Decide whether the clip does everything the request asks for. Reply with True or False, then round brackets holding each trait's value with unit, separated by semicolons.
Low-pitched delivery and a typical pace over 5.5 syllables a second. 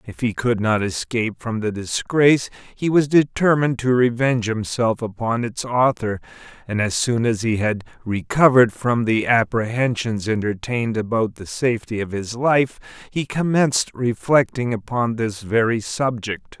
False (120 Hz; 4.7 syllables/s)